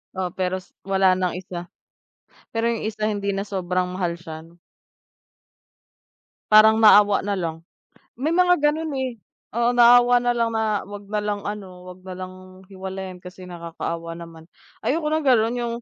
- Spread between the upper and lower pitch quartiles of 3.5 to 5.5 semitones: Yes, average, 4.2 semitones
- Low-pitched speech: No, high, 200 Hz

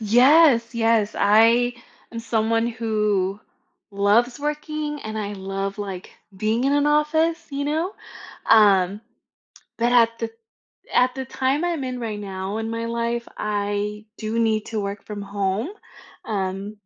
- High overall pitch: Yes, high, 225 Hz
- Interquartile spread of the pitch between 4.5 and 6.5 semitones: No, average, 3.5 semitones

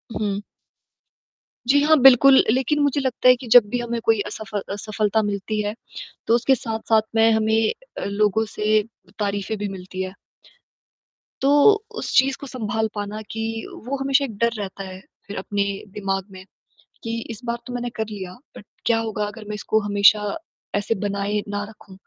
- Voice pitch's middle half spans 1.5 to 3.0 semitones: Yes, average, 2.7 semitones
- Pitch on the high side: Yes, high, 215 Hz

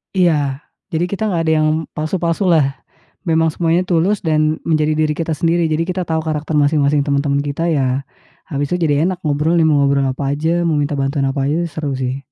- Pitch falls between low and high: Yes, medium, 155 Hz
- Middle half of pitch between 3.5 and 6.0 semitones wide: No, narrow, 2.6 semitones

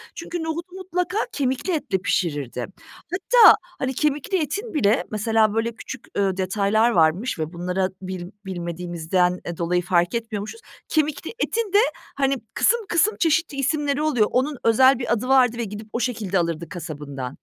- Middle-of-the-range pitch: No, high, 230 Hz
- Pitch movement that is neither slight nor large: No, wide, 8.8 semitones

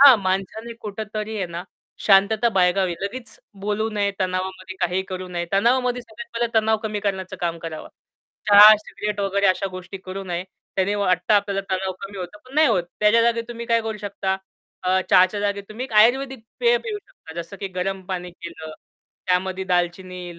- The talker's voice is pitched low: No, high, 200 Hz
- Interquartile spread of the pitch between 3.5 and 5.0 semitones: No, average, 3.0 semitones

